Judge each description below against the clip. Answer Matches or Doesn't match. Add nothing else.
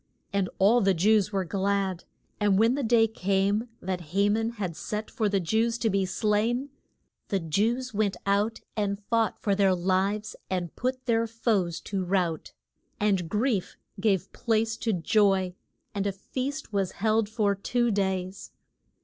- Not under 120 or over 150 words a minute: Doesn't match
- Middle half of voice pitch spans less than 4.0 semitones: Matches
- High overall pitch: Matches